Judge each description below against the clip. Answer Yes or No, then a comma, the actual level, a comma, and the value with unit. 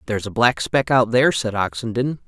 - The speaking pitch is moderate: No, low, 120 Hz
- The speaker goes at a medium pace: No, fast, 210 wpm